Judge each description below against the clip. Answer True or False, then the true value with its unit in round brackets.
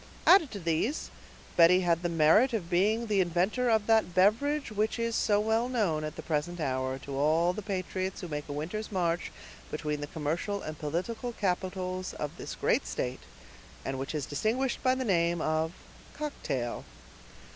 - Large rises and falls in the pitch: True (5.7 semitones)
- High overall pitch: False (180 Hz)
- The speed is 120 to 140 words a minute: False (175 wpm)